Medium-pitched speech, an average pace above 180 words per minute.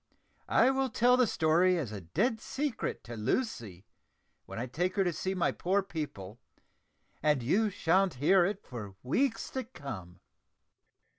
No: medium, 175 Hz; average, 155 wpm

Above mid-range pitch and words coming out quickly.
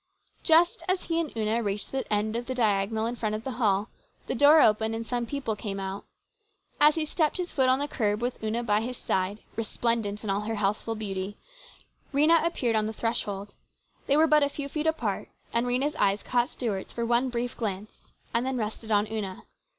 Yes: high, 230 Hz; fast, 210 wpm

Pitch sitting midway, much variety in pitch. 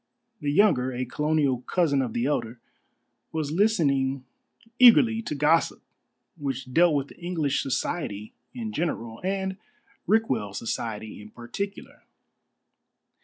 Yes: medium, 145 Hz; wide, 6.0 semitones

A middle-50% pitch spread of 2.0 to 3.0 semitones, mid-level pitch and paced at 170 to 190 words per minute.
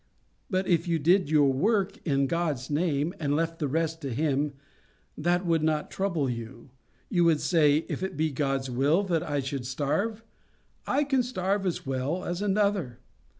No: average, 4.7 semitones; medium, 160 Hz; average, 175 wpm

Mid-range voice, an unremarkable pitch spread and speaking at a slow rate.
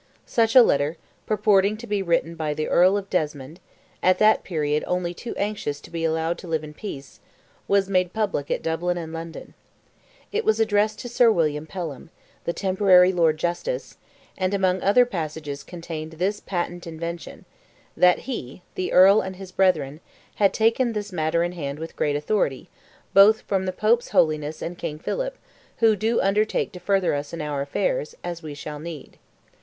No: medium, 180 Hz; average, 4.5 semitones; average, 170 wpm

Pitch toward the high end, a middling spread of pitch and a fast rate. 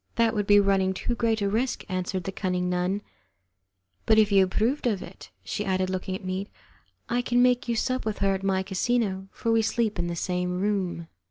Yes: high, 200 Hz; average, 3.2 semitones; fast, 210 wpm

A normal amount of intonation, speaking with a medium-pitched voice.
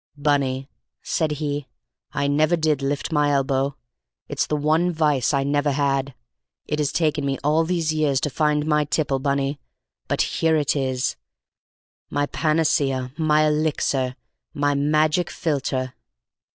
No: narrow, 1.9 semitones; medium, 145 Hz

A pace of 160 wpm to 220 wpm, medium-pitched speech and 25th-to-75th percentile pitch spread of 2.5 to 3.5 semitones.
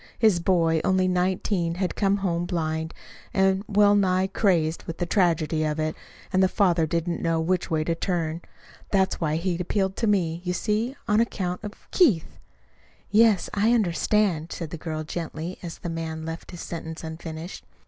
Yes: average, 180 wpm; medium, 175 Hz; average, 2.9 semitones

